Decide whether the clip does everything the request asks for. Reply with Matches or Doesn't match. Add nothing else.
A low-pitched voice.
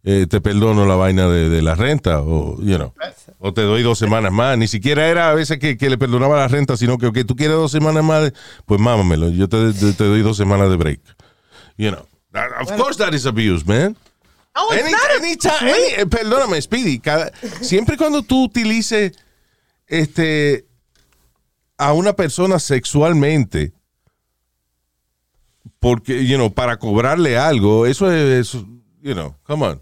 Matches